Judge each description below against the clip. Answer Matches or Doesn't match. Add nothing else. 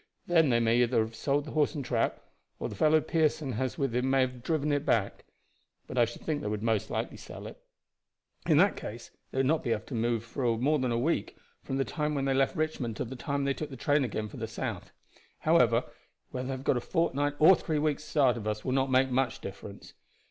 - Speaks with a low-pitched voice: Matches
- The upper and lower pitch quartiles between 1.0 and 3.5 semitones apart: Doesn't match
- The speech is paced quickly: Matches